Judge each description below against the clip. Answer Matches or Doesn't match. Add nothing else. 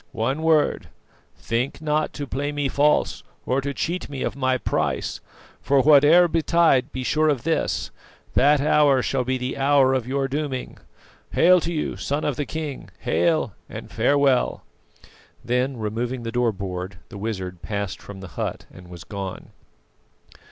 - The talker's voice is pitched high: Doesn't match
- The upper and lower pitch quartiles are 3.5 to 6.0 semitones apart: Matches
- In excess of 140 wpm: Matches